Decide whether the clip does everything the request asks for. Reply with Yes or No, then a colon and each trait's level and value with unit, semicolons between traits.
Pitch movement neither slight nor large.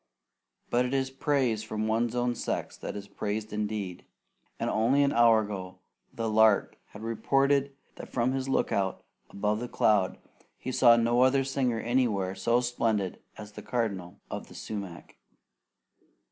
Yes: average, 3.2 semitones